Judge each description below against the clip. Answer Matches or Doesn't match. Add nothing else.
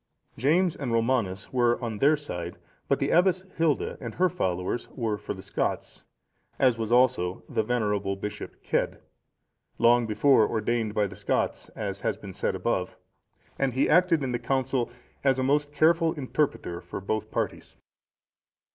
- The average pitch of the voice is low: Matches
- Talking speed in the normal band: Matches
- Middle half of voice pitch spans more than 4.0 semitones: Matches